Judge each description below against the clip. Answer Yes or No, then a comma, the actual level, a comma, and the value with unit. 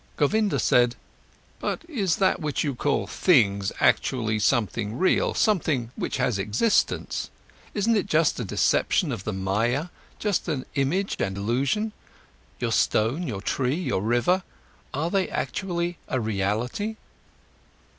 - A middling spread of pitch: No, wide, 8.4 semitones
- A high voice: No, low, 135 Hz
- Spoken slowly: Yes, slow, 130 wpm